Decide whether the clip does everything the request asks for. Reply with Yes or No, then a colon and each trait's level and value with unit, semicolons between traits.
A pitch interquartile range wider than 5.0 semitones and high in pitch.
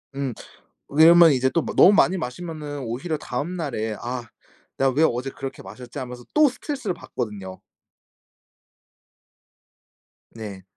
No: wide, 5.4 semitones; low, 135 Hz